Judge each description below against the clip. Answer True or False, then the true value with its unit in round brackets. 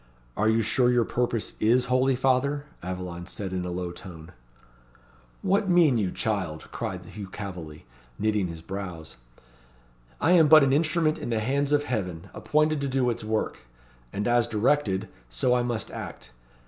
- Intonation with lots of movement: True (6.5 semitones)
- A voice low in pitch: True (115 Hz)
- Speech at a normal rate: True (165 wpm)